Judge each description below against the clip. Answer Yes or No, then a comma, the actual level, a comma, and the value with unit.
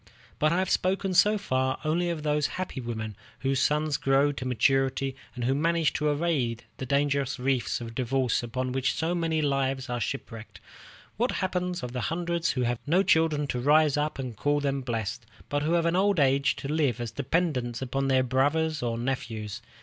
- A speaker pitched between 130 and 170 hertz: Yes, medium, 140 Hz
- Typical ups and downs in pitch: Yes, average, 4.1 semitones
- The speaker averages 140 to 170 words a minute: No, average, 195 wpm